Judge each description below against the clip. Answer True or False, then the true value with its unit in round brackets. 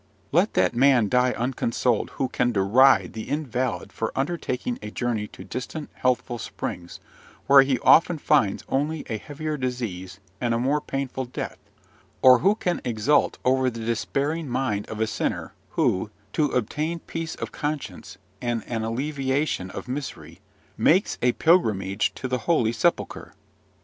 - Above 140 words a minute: True (150 wpm)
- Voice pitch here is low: True (125 Hz)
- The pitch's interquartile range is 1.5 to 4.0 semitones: False (4.5 semitones)